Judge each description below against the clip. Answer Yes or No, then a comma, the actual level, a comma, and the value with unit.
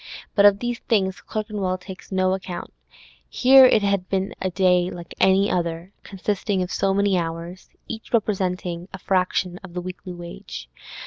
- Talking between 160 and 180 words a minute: Yes, average, 165 wpm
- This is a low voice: No, high, 190 Hz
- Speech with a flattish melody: Yes, narrow, 1.9 semitones